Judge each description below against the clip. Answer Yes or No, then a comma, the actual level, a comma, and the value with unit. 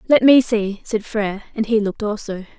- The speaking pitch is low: No, high, 215 Hz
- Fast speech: Yes, fast, 210 wpm